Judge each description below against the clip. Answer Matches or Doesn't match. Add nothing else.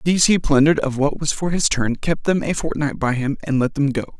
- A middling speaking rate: Doesn't match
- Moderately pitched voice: Matches